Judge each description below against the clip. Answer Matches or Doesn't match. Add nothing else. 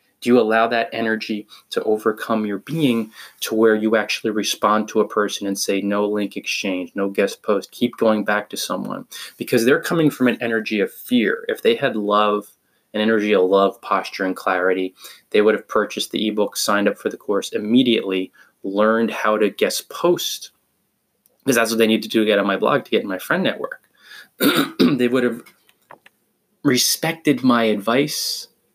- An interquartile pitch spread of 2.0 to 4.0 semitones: Matches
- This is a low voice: Matches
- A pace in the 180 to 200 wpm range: Matches